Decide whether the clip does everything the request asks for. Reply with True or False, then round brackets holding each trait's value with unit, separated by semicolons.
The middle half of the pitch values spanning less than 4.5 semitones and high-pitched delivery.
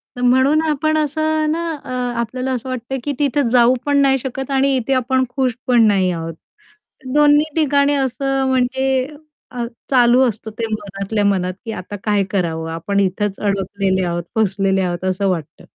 False (5.5 semitones; 245 Hz)